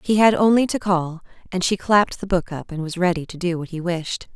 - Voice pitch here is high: No, medium, 180 Hz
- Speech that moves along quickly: Yes, fast, 260 wpm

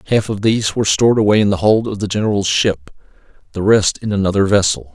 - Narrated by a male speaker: Yes, male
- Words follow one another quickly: Yes, fast, 220 wpm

